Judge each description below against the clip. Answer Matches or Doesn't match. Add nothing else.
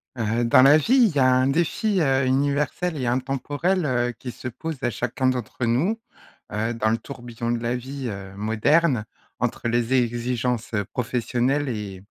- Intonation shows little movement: Doesn't match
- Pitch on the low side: Matches